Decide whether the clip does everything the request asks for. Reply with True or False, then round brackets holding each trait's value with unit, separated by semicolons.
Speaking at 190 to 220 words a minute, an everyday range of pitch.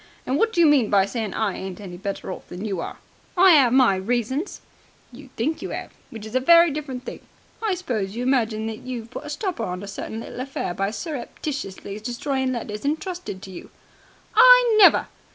False (205 wpm; 6.2 semitones)